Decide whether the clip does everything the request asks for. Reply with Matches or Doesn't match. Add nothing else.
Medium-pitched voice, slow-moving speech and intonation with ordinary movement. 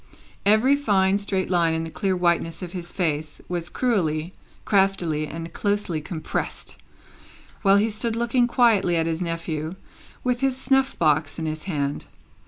Doesn't match